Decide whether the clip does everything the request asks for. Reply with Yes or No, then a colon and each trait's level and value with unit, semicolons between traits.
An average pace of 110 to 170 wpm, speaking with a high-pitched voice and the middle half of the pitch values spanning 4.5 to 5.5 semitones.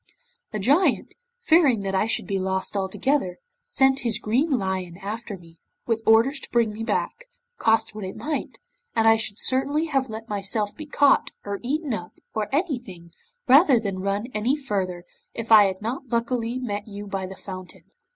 No: average, 180 wpm; high, 220 Hz; average, 5.2 semitones